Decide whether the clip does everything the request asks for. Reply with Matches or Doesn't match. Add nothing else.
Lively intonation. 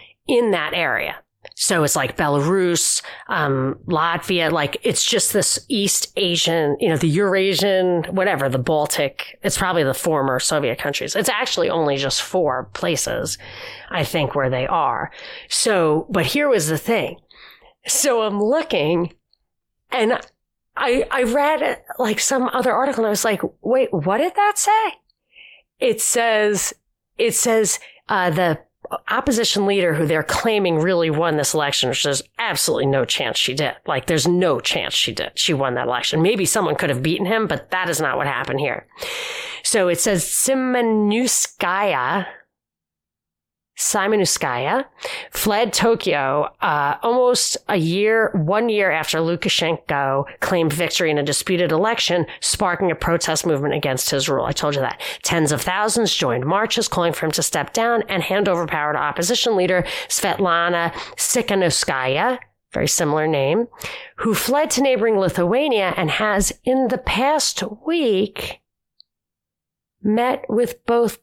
Matches